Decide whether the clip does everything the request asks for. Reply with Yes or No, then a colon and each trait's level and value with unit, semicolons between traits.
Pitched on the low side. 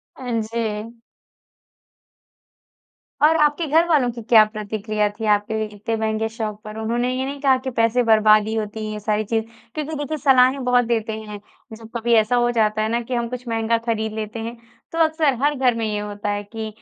No: high, 225 Hz